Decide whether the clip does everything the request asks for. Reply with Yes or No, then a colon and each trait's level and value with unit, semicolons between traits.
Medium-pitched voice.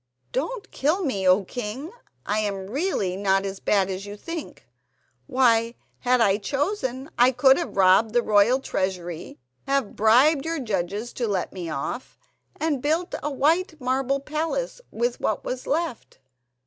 No: high, 245 Hz